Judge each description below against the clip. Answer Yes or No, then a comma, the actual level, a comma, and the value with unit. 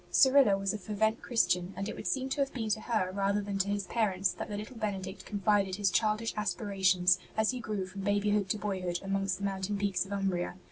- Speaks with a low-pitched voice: No, high, 200 Hz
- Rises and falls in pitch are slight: Yes, narrow, 1.9 semitones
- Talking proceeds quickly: Yes, fast, 225 wpm